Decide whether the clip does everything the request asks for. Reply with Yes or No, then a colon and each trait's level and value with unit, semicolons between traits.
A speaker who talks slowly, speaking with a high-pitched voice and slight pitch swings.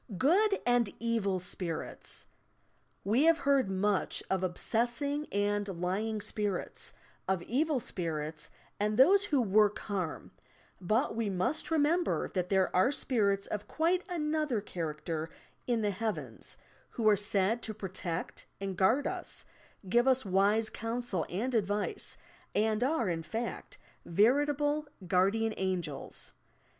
No: slow, 130 wpm; high, 215 Hz; average, 5.2 semitones